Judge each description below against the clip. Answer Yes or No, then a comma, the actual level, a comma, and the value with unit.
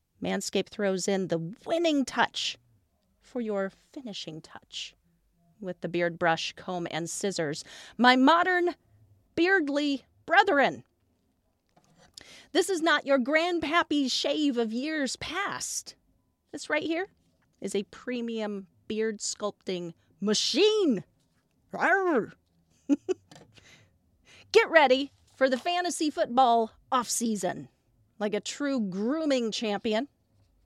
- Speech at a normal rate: No, slow, 100 wpm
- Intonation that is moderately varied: No, wide, 8.7 semitones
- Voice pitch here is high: Yes, high, 230 Hz